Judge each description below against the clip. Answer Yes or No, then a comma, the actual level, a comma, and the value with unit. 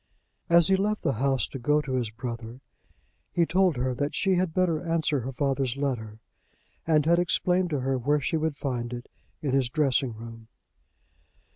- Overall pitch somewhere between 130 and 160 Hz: Yes, medium, 140 Hz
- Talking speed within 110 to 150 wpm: No, average, 180 wpm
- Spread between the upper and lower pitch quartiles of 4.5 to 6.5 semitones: Yes, average, 4.9 semitones